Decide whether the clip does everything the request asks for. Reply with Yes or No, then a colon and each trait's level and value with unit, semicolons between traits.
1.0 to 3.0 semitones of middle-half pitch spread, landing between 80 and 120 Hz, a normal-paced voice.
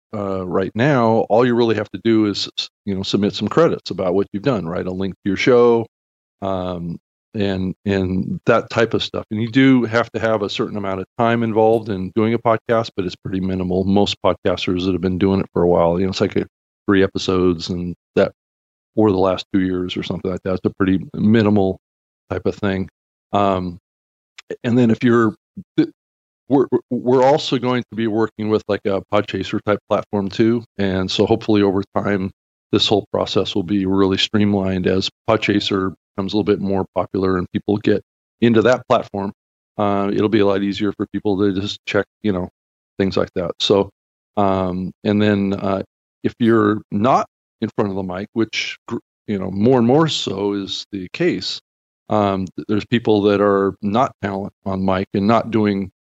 Yes: narrow, 2.6 semitones; low, 100 Hz; average, 195 wpm